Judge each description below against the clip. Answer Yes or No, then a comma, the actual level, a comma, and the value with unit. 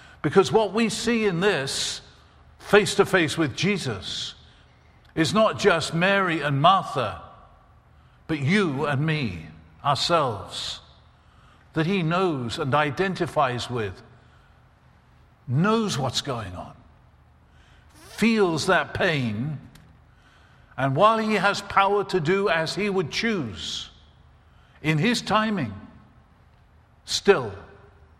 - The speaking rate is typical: No, slow, 105 wpm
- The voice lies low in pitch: No, medium, 160 Hz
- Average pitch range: No, wide, 8.3 semitones